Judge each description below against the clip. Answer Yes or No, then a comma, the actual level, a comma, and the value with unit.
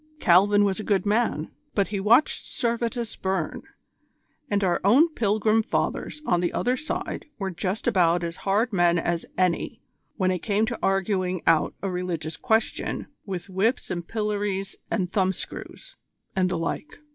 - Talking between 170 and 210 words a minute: No, average, 160 wpm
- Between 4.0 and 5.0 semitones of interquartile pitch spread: No, average, 3.4 semitones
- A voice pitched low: No, high, 195 Hz